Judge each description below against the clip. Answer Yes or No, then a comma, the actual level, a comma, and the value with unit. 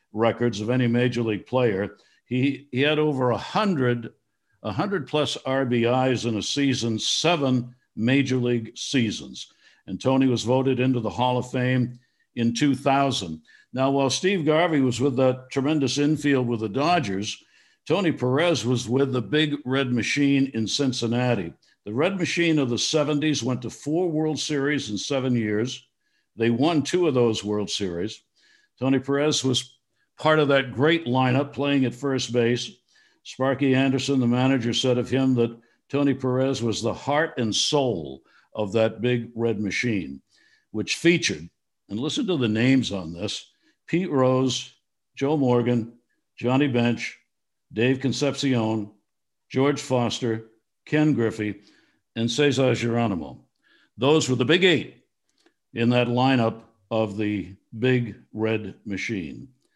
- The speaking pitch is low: Yes, low, 125 Hz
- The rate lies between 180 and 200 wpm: No, average, 145 wpm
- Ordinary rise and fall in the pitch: Yes, average, 3.1 semitones